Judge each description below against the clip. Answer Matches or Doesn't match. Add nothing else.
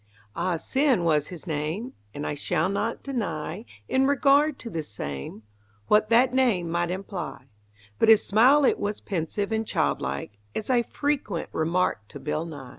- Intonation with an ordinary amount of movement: Doesn't match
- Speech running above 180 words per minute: Doesn't match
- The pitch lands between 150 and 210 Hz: Matches